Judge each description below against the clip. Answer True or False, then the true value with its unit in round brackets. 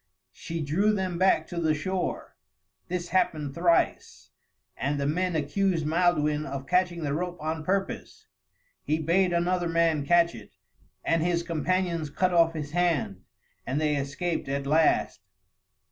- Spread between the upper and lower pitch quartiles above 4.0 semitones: False (2.9 semitones)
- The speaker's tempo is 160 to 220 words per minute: False (145 wpm)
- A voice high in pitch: False (165 Hz)